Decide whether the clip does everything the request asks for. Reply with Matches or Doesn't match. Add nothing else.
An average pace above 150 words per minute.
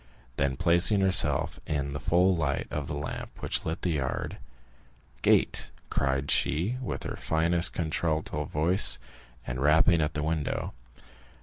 Doesn't match